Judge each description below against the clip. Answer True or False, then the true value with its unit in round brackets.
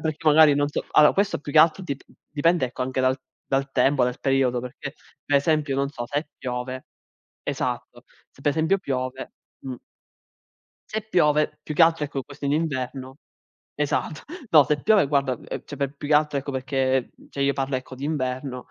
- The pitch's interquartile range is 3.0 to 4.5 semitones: False (2.6 semitones)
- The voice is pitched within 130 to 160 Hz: True (140 Hz)